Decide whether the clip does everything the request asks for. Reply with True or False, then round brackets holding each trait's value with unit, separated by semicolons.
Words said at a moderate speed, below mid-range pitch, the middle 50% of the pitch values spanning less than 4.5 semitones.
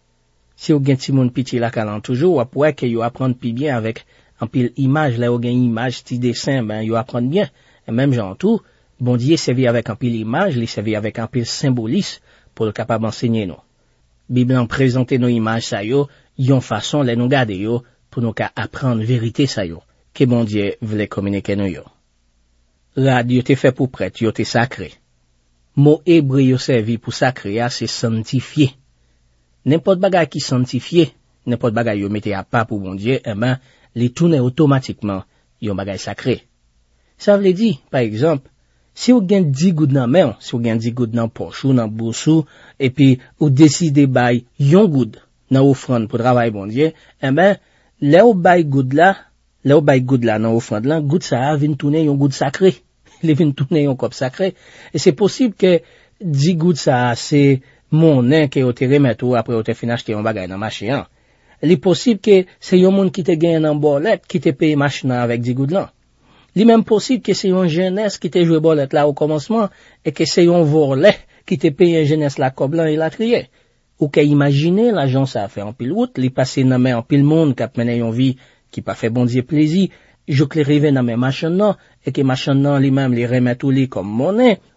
False (205 wpm; 130 Hz; 4.8 semitones)